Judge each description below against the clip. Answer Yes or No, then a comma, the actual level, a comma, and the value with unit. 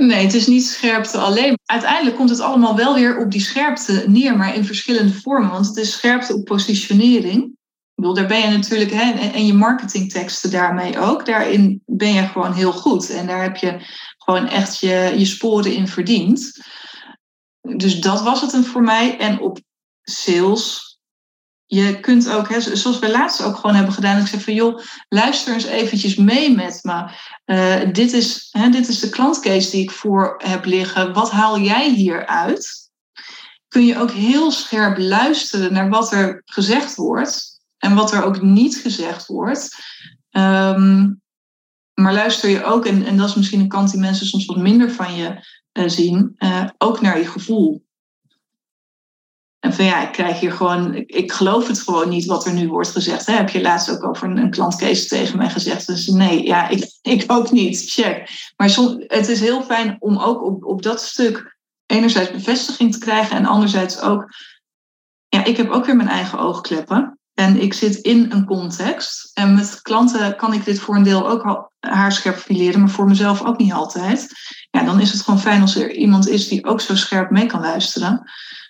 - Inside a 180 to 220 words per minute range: Yes, average, 195 wpm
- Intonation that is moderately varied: Yes, average, 3.3 semitones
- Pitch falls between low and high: No, high, 210 Hz